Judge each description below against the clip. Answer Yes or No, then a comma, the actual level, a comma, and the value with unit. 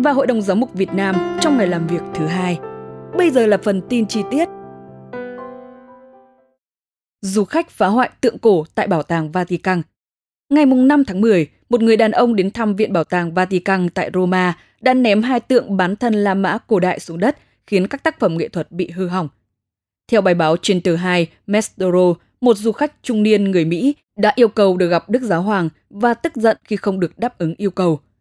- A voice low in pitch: No, high, 195 Hz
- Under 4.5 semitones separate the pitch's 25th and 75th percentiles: No, average, 5.0 semitones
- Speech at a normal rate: No, fast, 215 wpm